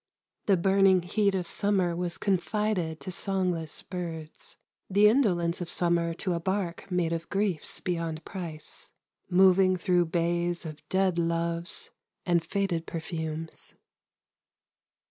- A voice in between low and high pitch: Yes, medium, 175 Hz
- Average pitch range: No, narrow, 2.3 semitones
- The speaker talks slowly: Yes, slow, 125 wpm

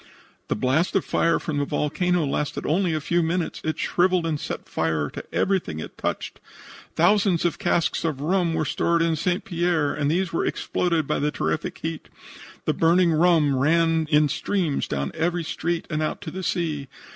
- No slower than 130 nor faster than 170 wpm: No, average, 185 wpm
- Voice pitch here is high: No, medium, 165 Hz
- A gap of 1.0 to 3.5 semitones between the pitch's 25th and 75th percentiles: Yes, average, 2.9 semitones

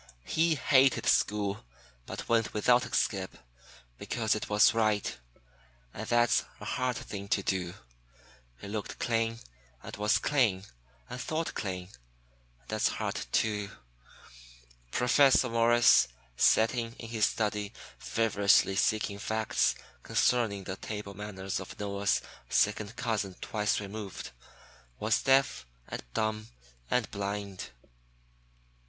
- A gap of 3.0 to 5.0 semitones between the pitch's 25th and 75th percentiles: No, narrow, 2.5 semitones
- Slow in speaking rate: Yes, slow, 120 wpm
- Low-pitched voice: Yes, low, 105 Hz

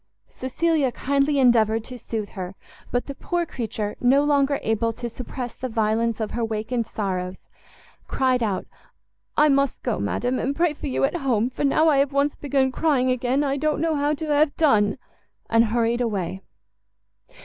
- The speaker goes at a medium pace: Yes, average, 175 wpm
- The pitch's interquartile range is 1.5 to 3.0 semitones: No, average, 4.0 semitones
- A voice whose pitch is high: Yes, very high, 255 Hz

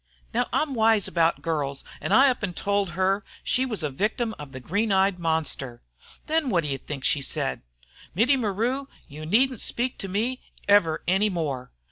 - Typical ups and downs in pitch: No, wide, 6.2 semitones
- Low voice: No, high, 195 Hz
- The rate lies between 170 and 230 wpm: Yes, average, 180 wpm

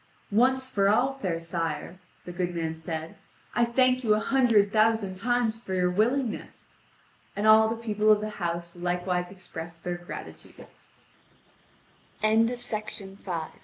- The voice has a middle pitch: No, high, 205 Hz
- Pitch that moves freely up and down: No, average, 4.3 semitones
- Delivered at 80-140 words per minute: Yes, slow, 135 wpm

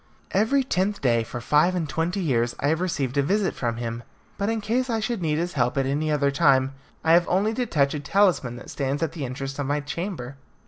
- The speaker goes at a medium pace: No, fast, 235 wpm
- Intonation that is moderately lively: No, wide, 6.0 semitones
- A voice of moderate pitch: Yes, medium, 150 Hz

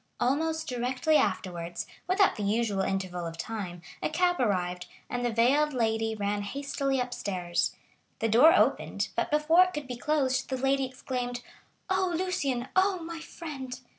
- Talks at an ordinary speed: Yes, average, 150 wpm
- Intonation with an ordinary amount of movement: No, wide, 6.5 semitones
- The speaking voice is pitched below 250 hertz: No, very high, 255 Hz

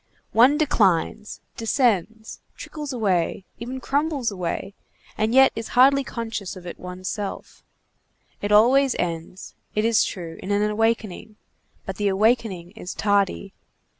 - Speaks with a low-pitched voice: No, high, 215 Hz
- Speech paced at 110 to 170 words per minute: Yes, slow, 135 wpm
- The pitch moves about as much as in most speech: Yes, average, 4.0 semitones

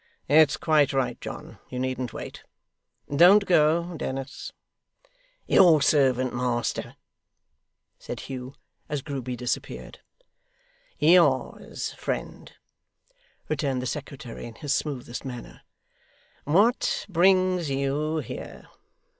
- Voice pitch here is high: No, medium, 140 Hz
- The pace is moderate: No, slow, 95 wpm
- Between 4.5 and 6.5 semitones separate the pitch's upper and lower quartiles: No, average, 3.8 semitones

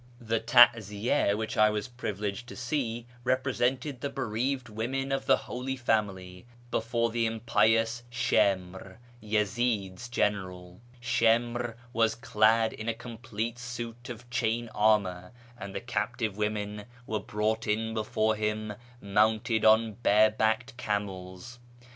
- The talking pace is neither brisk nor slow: No, slow, 125 wpm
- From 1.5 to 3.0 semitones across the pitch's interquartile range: Yes, narrow, 2.4 semitones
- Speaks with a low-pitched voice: Yes, low, 110 Hz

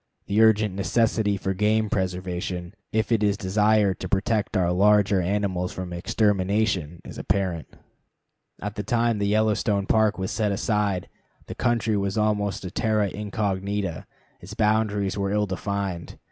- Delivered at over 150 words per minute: No, average, 145 wpm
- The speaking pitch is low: Yes, low, 100 Hz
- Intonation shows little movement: Yes, narrow, 2.2 semitones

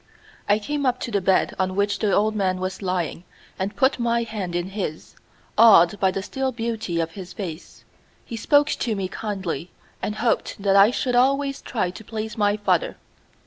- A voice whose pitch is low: No, high, 205 Hz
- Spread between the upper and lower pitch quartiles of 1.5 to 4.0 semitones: Yes, average, 3.7 semitones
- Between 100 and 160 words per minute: No, average, 190 wpm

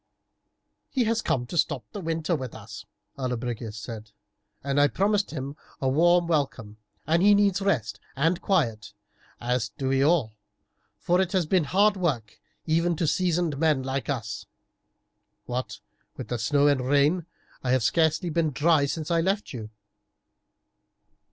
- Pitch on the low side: No, medium, 150 Hz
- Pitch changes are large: Yes, wide, 5.7 semitones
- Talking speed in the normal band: Yes, average, 150 wpm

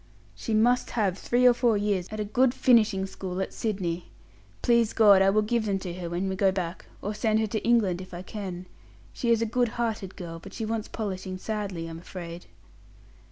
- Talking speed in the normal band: No, fast, 210 wpm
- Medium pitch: No, high, 205 Hz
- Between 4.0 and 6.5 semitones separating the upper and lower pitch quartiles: No, average, 3.3 semitones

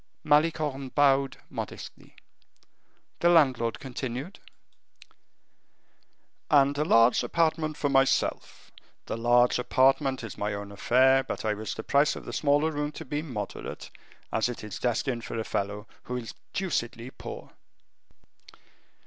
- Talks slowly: Yes, slow, 130 wpm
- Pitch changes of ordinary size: Yes, average, 4.0 semitones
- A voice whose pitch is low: Yes, low, 130 Hz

